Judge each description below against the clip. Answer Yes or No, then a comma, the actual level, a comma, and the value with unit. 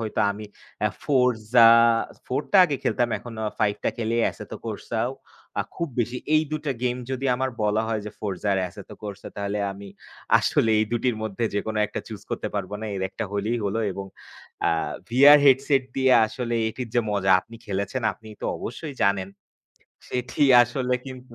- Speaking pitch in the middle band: No, low, 115 Hz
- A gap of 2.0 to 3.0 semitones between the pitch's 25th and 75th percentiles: No, average, 3.5 semitones